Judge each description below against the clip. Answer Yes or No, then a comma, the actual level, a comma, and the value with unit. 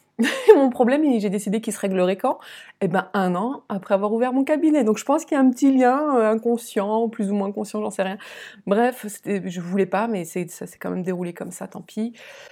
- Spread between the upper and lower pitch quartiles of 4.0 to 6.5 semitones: Yes, average, 4.4 semitones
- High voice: Yes, high, 215 Hz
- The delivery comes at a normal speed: No, fast, 235 wpm